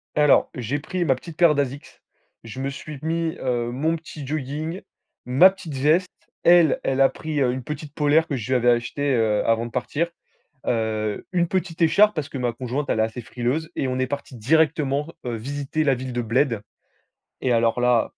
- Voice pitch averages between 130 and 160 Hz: Yes, medium, 140 Hz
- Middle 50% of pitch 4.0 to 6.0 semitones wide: Yes, average, 4.3 semitones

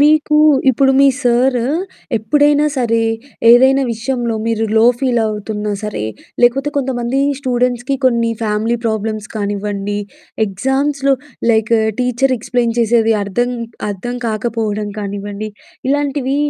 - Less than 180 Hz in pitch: No, high, 235 Hz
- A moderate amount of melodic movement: Yes, average, 3.7 semitones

